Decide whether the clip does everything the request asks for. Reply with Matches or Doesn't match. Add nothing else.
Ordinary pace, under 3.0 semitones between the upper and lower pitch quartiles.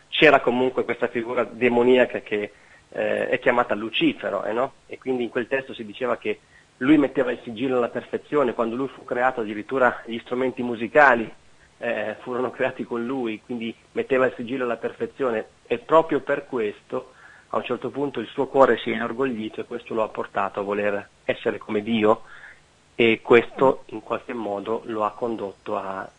Doesn't match